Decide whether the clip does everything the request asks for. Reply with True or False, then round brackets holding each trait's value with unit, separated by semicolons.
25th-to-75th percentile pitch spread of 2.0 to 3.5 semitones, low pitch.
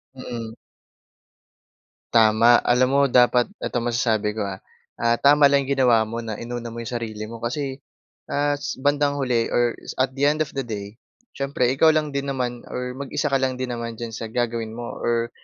True (2.9 semitones; 120 Hz)